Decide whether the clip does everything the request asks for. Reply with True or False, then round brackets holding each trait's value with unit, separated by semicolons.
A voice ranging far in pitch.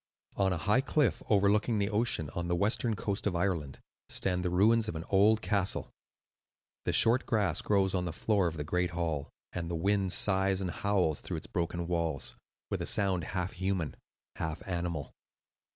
False (3.1 semitones)